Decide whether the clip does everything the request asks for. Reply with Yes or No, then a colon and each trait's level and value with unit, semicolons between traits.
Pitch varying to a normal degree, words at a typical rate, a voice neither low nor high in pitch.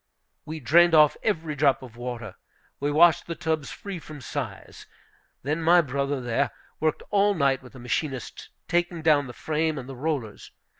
Yes: average, 3.6 semitones; average, 170 wpm; medium, 150 Hz